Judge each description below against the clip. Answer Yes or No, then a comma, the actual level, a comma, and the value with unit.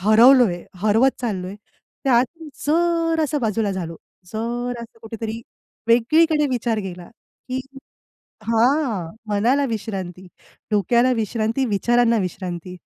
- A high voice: Yes, high, 230 Hz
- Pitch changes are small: No, average, 4.0 semitones